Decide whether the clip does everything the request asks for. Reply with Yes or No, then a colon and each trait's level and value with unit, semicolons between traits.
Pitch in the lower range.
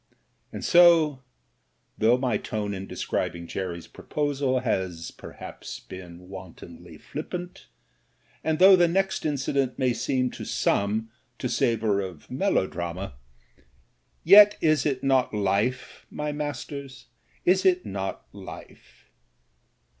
Yes: low, 125 Hz